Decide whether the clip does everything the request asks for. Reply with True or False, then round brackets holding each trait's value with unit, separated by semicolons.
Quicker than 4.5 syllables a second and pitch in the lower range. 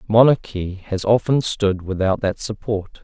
False (4.2 syllables/s; 105 Hz)